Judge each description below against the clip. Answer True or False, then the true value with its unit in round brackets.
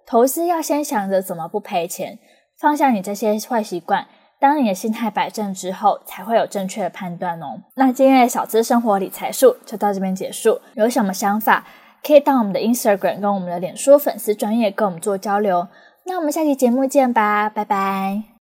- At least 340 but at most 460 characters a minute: False (330 characters per minute)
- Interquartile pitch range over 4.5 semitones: True (5.3 semitones)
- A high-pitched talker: True (215 Hz)